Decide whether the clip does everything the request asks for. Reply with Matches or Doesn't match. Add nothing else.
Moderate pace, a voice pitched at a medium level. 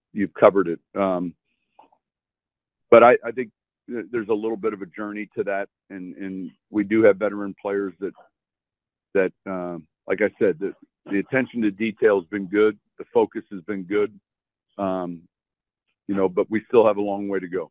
Doesn't match